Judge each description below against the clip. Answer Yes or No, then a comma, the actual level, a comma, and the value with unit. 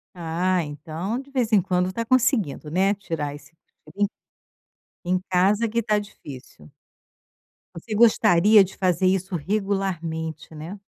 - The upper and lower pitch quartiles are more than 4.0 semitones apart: Yes, average, 4.5 semitones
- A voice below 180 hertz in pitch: No, medium, 185 Hz